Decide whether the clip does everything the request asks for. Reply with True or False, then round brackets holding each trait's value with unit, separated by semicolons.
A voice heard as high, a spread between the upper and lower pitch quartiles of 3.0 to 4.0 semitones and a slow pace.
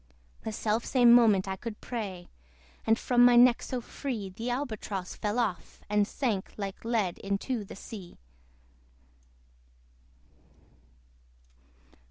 True (220 Hz; 3.5 semitones; 120 wpm)